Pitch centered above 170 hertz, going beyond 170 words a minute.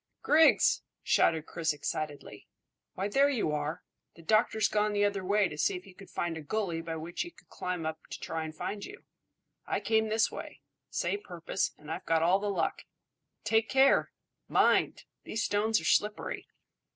Yes: high, 190 Hz; average, 185 wpm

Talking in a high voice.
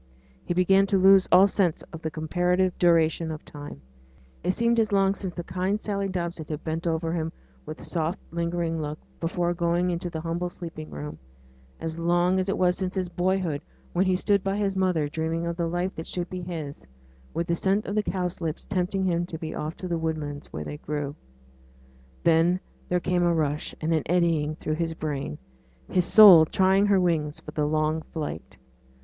No: medium, 170 Hz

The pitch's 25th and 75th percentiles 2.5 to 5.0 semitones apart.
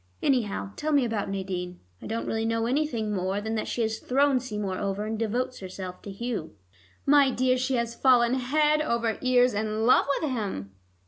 Yes: average, 3.7 semitones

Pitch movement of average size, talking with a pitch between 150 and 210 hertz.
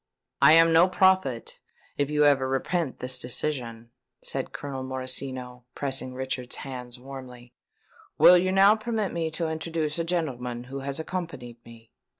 No: average, 4.7 semitones; low, 135 Hz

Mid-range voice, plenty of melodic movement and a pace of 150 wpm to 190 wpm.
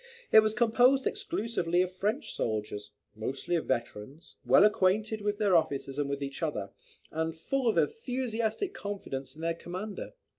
Yes: medium, 180 Hz; wide, 7.8 semitones; average, 155 wpm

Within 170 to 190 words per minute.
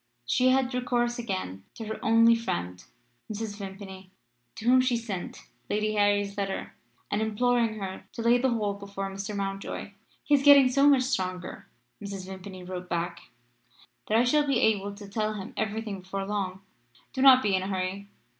Yes: average, 180 wpm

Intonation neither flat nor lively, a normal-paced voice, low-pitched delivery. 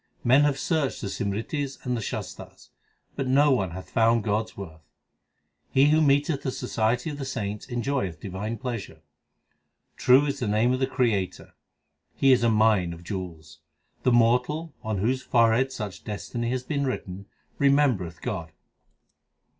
Yes: average, 4.8 semitones; average, 160 wpm; low, 120 Hz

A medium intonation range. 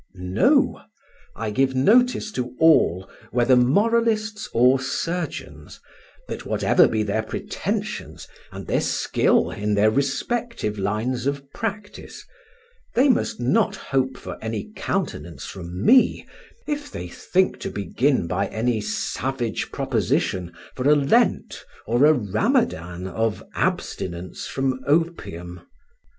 No: wide, 8.9 semitones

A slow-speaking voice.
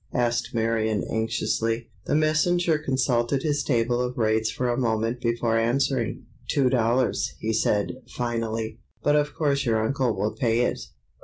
No: average, 150 wpm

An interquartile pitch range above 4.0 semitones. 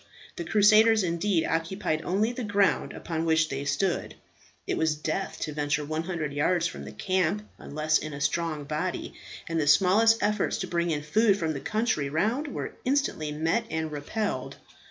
Yes: average, 5.2 semitones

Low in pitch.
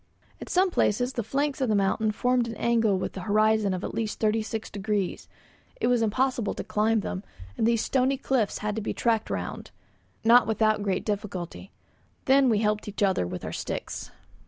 No: high, 220 Hz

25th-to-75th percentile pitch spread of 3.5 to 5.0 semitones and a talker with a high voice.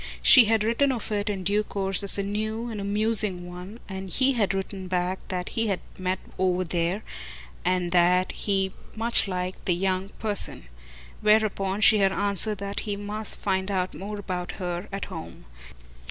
No: narrow, 2.4 semitones; high, 195 Hz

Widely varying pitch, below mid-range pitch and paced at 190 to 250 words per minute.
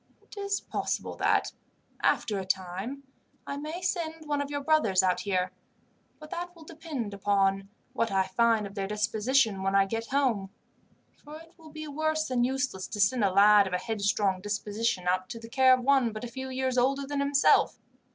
No: wide, 6.3 semitones; high, 235 Hz; average, 195 wpm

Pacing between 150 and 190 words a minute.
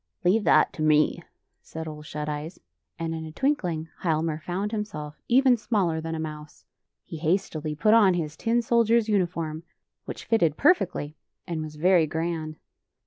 Yes: average, 170 wpm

